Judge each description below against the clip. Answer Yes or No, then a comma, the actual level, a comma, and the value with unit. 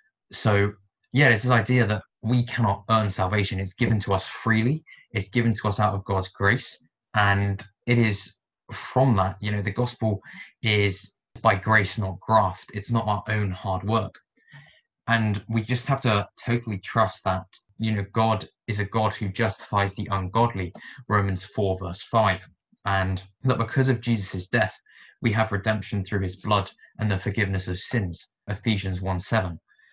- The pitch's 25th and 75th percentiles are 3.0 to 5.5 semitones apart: No, narrow, 2.6 semitones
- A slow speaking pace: No, average, 170 wpm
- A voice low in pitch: Yes, low, 105 Hz